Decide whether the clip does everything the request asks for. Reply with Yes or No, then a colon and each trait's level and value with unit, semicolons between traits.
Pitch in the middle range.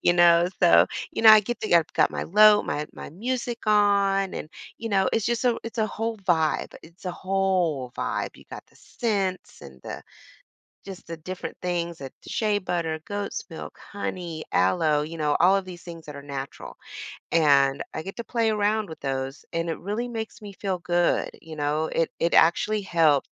Yes: medium, 180 Hz